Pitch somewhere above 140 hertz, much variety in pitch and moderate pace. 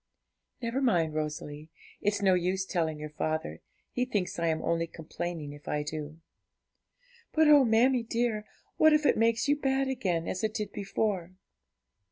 Yes: high, 190 Hz; wide, 6.9 semitones; average, 165 wpm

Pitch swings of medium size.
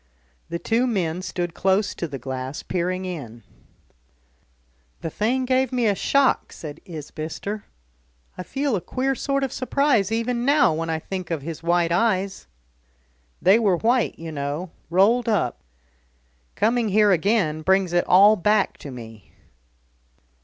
No: wide, 5.8 semitones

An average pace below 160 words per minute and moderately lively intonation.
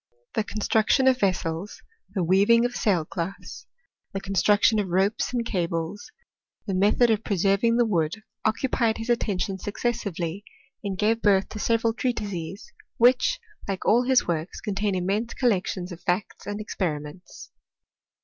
Yes: average, 150 wpm; average, 3.7 semitones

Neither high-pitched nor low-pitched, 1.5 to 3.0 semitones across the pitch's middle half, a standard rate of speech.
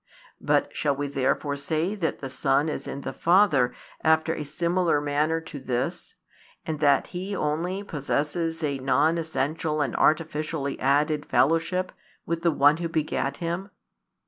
Yes: medium, 155 Hz; average, 2.7 semitones; average, 150 wpm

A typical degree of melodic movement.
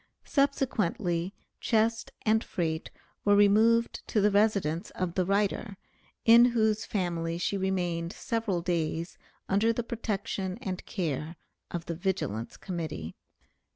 Yes: average, 4.3 semitones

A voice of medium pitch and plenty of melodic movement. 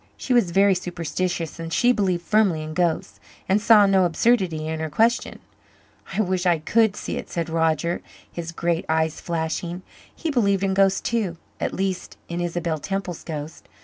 No: medium, 175 Hz; average, 3.1 semitones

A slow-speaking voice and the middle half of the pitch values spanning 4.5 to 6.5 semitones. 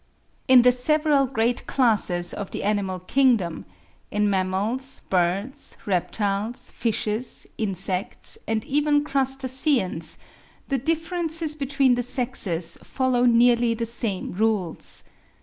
Yes: slow, 100 wpm; average, 5.2 semitones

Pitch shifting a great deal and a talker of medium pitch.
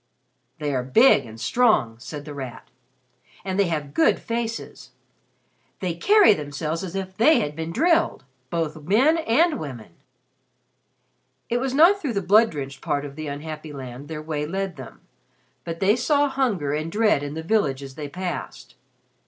Yes: wide, 7.6 semitones; medium, 165 Hz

